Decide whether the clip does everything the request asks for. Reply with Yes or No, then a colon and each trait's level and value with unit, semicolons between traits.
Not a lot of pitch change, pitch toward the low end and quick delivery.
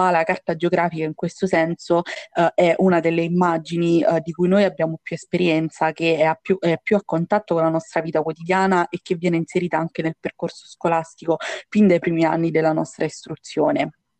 No: narrow, 1.5 semitones; medium, 170 Hz; fast, 190 wpm